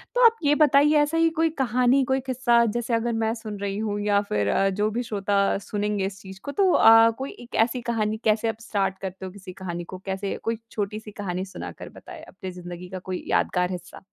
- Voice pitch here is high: Yes, high, 210 Hz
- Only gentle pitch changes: No, average, 3.9 semitones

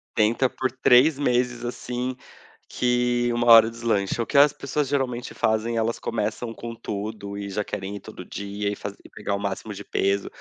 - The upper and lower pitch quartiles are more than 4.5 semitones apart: No, average, 3.1 semitones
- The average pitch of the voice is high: No, low, 115 Hz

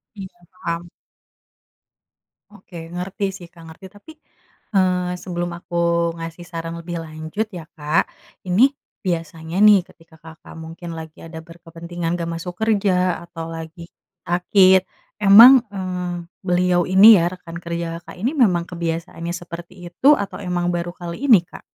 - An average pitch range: No, narrow, 1.9 semitones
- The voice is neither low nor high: Yes, medium, 175 Hz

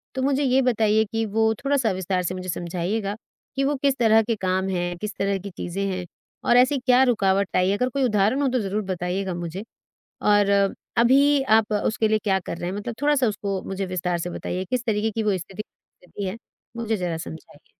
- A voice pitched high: Yes, high, 205 Hz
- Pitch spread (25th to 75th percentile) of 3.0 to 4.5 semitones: Yes, average, 4.0 semitones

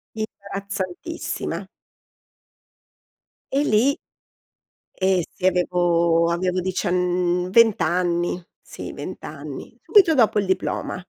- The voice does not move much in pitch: No, average, 3.2 semitones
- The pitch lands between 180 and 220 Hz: Yes, medium, 185 Hz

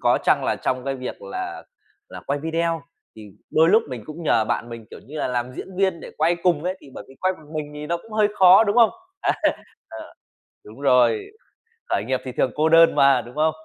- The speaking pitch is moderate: Yes, medium, 155 Hz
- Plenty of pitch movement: Yes, wide, 5.7 semitones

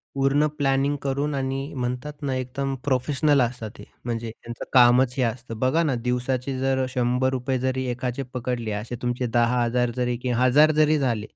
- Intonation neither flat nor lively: No, narrow, 1.9 semitones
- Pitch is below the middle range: Yes, low, 130 Hz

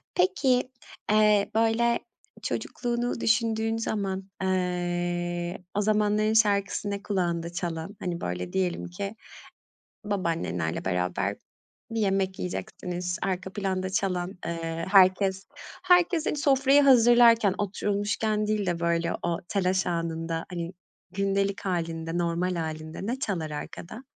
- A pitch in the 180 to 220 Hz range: Yes, high, 190 Hz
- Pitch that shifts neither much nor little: Yes, average, 3.6 semitones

